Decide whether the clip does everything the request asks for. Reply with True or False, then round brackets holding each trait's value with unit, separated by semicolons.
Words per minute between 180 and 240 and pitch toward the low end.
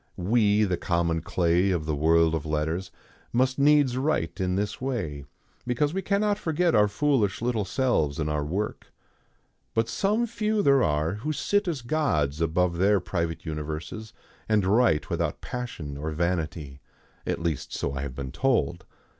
False (165 wpm; 95 Hz)